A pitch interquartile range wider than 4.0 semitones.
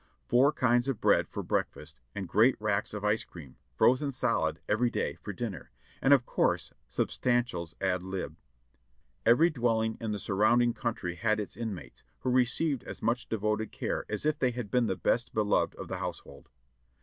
No: average, 3.5 semitones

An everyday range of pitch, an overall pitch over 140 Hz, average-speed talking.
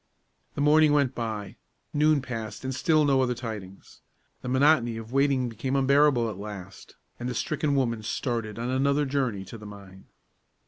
No: average, 4.2 semitones; low, 125 Hz; average, 170 wpm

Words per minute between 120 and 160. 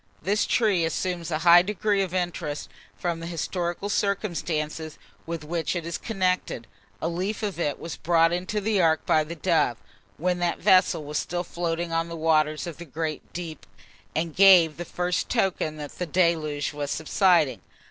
No: average, 175 wpm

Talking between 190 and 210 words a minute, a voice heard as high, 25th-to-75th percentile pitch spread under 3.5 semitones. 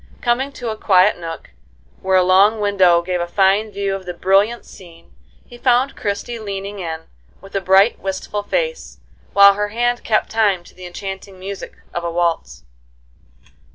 No: average, 170 wpm; high, 195 Hz; average, 2.8 semitones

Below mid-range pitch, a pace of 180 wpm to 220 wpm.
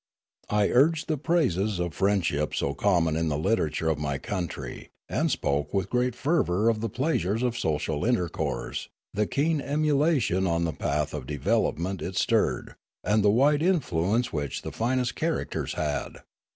No: low, 100 Hz; average, 170 wpm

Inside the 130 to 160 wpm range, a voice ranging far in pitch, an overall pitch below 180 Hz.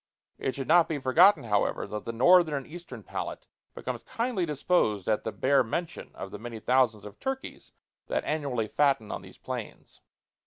No: average, 180 wpm; wide, 7.2 semitones; low, 135 Hz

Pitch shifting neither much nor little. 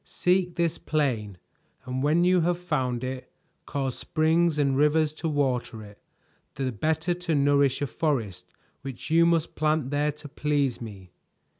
Yes: average, 3.8 semitones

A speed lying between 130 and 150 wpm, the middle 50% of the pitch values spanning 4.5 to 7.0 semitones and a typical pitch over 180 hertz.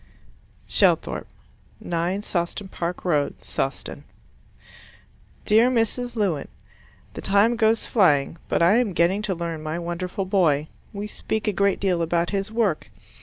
No: slow, 135 wpm; average, 3.7 semitones; high, 190 Hz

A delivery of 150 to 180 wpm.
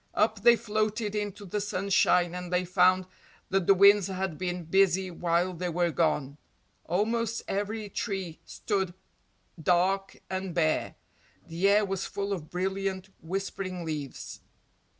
No: slow, 135 wpm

